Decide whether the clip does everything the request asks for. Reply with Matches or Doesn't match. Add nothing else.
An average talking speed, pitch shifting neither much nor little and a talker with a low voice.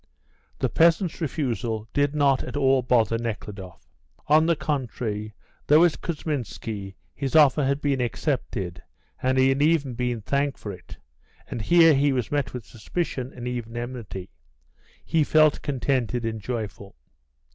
Matches